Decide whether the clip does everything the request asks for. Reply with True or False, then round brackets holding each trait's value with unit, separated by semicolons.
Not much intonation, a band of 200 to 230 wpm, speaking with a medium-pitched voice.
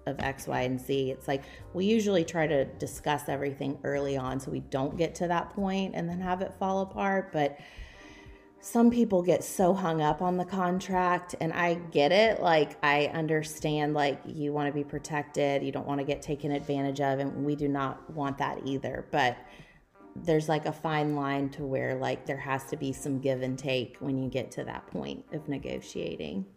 False (3.4 semitones; 205 wpm; 145 Hz)